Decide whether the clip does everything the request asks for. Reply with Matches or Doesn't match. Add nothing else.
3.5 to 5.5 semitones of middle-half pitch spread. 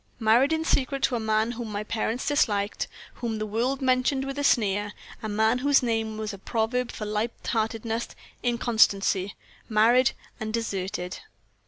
Doesn't match